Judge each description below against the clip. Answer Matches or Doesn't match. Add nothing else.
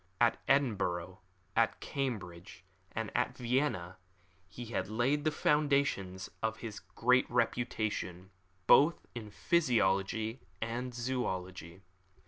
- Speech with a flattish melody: Doesn't match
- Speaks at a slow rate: Matches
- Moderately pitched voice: Doesn't match